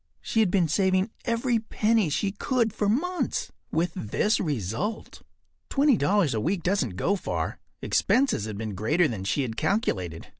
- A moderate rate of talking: Yes, average, 160 wpm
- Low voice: No, medium, 185 Hz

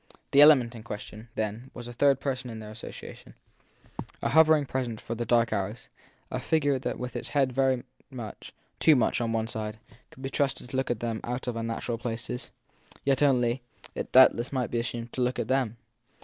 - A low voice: Yes, low, 120 Hz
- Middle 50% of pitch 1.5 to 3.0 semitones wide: Yes, narrow, 2.6 semitones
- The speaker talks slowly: No, average, 200 wpm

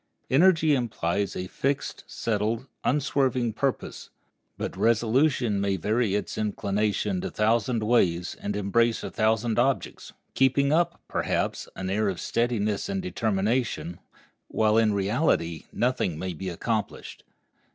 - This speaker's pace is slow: Yes, slow, 130 wpm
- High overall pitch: No, low, 110 Hz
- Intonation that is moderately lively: Yes, average, 4.0 semitones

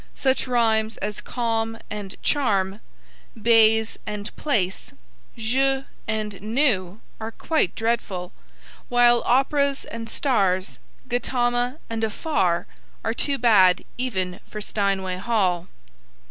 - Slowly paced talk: Yes, slow, 105 wpm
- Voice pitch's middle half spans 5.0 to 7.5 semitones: No, average, 3.7 semitones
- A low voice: No, high, 225 Hz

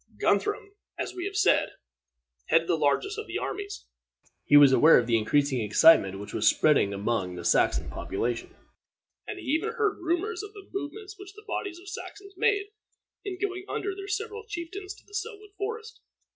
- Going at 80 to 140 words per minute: No, average, 175 wpm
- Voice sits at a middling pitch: No, very high, 385 Hz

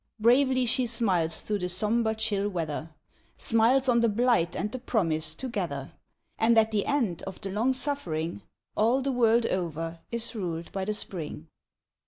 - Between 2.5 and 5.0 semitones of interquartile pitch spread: No, wide, 5.4 semitones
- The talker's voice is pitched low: No, high, 215 Hz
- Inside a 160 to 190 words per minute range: Yes, average, 165 wpm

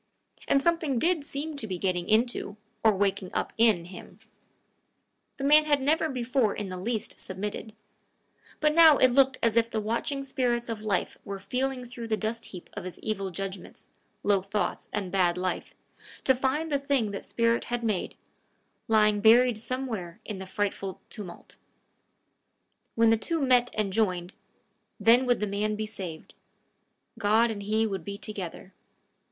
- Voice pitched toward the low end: No, high, 220 Hz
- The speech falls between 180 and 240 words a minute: No, average, 165 wpm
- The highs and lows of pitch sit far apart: No, average, 4.3 semitones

